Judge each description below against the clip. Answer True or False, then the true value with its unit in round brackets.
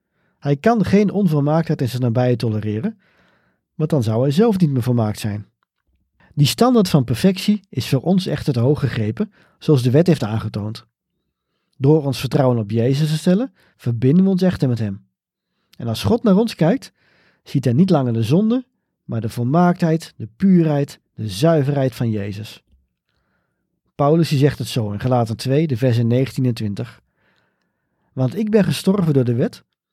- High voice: False (140 Hz)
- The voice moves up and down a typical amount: False (6.6 semitones)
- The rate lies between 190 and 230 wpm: False (170 wpm)